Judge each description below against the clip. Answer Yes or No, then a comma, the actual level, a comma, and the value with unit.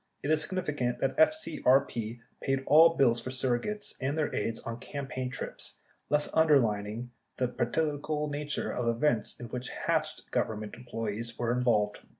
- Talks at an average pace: Yes, average, 155 wpm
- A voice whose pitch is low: Yes, low, 130 Hz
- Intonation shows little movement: No, average, 4.2 semitones